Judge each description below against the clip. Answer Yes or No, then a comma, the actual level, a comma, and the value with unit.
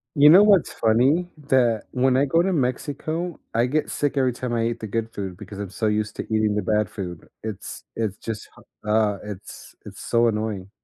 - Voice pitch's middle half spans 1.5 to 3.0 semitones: No, average, 4.1 semitones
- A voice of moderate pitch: No, low, 115 Hz